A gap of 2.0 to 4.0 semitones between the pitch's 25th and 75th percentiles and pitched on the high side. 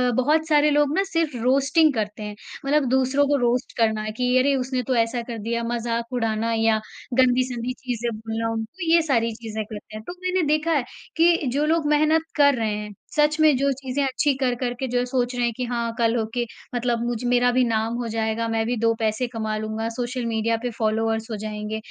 Yes: average, 3.4 semitones; high, 245 Hz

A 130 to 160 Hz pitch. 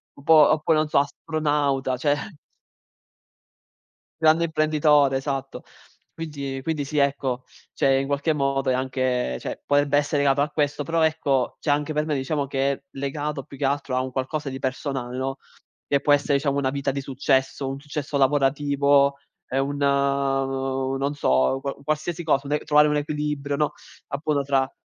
Yes: medium, 140 Hz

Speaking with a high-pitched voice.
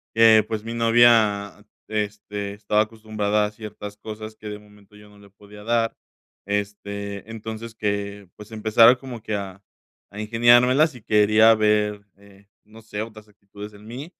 No: low, 105 Hz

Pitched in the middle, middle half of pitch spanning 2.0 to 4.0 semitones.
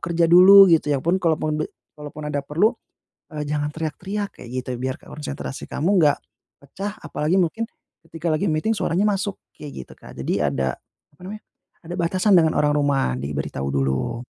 No: medium, 155 Hz; average, 4.5 semitones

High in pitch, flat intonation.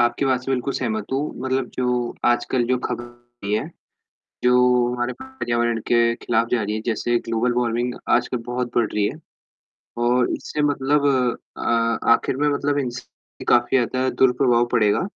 No: low, 125 Hz; narrow, 1.5 semitones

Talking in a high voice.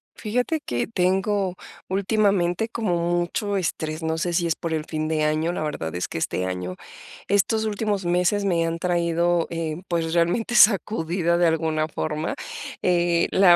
No: medium, 175 Hz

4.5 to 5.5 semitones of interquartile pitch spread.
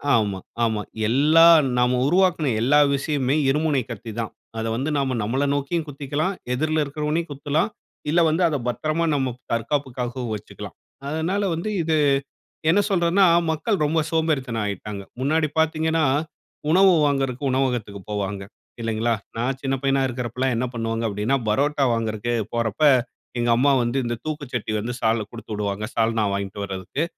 Yes: average, 5.2 semitones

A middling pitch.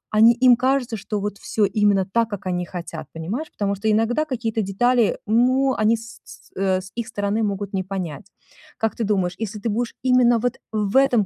No: high, 215 Hz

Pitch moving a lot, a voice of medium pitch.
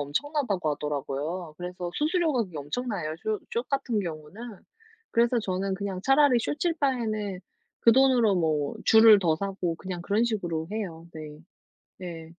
No: wide, 6.4 semitones; high, 195 Hz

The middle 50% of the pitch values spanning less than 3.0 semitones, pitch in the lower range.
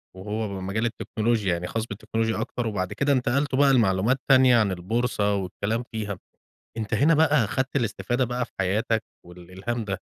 No: average, 3.7 semitones; low, 110 Hz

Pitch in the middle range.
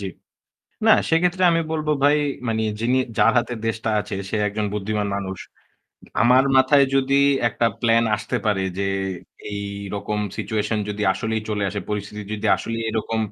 No: low, 110 Hz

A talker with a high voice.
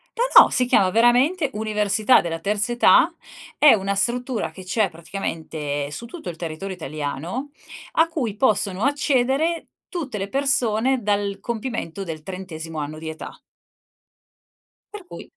Yes: high, 210 Hz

